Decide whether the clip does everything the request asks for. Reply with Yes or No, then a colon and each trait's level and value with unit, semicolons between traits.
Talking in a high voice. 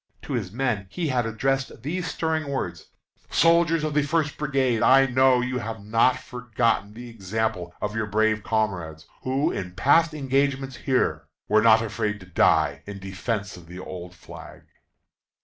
No: low, 115 Hz